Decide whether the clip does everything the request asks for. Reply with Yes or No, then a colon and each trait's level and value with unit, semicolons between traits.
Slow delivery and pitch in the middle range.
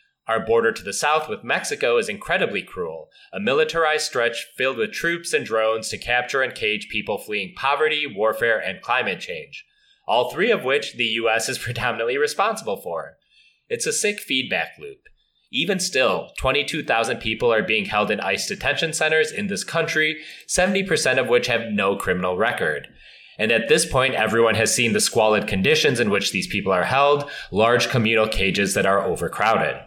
No: average, 175 wpm; medium, 155 Hz